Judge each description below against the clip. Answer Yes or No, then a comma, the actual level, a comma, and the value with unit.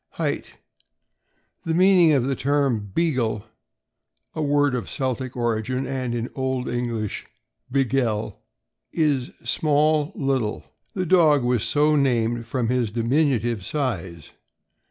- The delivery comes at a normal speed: No, slow, 120 wpm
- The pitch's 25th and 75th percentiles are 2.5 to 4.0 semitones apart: Yes, average, 3.7 semitones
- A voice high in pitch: No, low, 130 Hz